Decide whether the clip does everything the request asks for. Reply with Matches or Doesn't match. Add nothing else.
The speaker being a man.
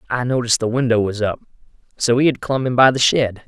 Matches